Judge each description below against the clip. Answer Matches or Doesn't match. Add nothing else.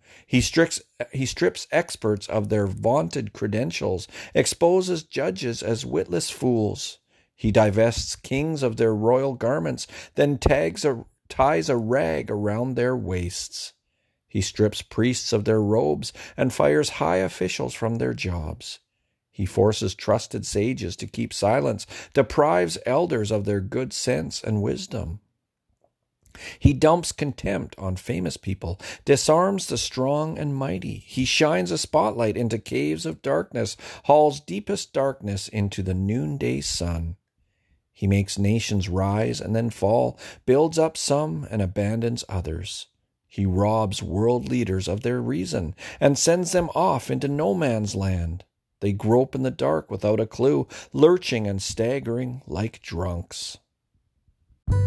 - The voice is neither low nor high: Doesn't match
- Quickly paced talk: Doesn't match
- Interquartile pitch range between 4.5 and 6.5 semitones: Matches